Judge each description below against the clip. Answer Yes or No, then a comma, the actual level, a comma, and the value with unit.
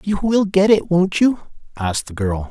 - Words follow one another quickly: Yes, fast, 215 wpm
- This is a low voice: No, medium, 165 Hz